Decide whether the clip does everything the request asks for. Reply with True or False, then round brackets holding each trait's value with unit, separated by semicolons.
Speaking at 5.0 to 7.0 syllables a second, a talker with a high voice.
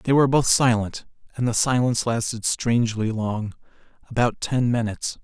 False (5.5 syllables/s; 115 Hz)